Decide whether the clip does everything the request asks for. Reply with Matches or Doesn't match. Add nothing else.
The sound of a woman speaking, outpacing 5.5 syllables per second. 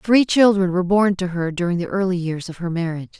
Matches